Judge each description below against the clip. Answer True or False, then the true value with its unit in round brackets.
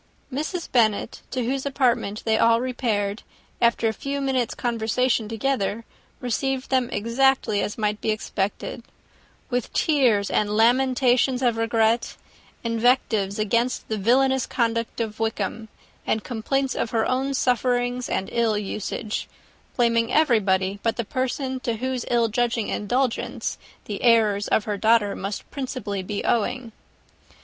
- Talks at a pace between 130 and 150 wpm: True (135 wpm)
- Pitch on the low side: False (230 Hz)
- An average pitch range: True (3.0 semitones)